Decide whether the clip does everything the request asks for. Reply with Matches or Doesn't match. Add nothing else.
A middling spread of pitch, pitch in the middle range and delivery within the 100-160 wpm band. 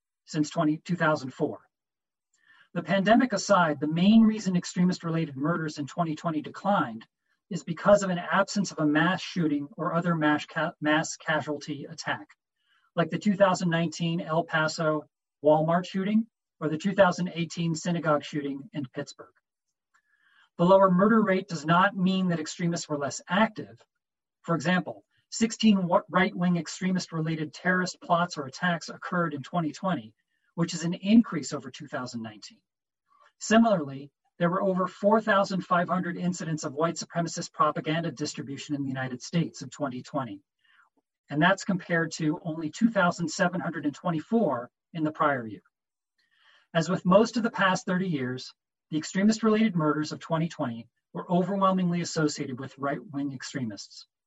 Matches